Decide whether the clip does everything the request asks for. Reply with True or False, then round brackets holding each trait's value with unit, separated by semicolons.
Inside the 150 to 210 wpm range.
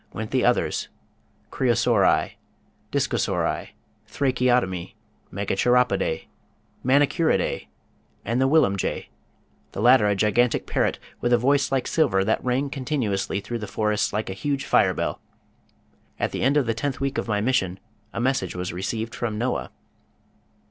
False (140 wpm)